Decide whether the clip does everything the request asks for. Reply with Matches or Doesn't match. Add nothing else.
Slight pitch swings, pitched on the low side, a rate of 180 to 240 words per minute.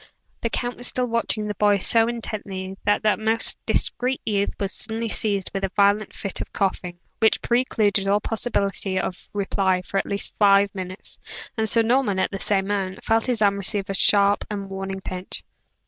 Doesn't match